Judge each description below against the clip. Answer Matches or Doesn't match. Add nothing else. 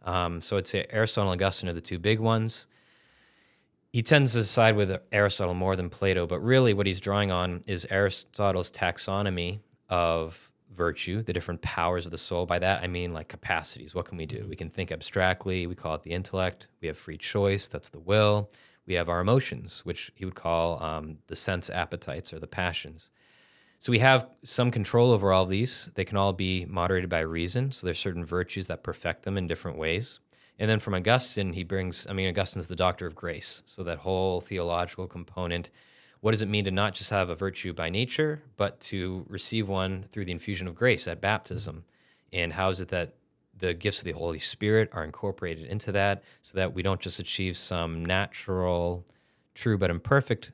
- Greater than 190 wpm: Matches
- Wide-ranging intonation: Doesn't match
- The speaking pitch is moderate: Doesn't match